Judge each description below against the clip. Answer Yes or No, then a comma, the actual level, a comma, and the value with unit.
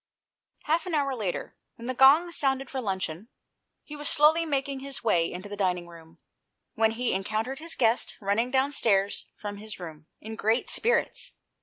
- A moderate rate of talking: Yes, average, 170 wpm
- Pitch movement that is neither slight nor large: No, wide, 5.7 semitones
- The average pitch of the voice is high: Yes, high, 230 Hz